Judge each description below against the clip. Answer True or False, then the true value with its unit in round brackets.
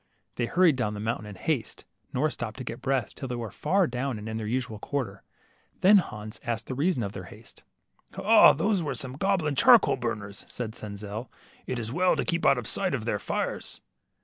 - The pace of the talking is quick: True (215 wpm)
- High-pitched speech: False (125 Hz)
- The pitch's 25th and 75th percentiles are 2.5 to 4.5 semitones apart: False (5.3 semitones)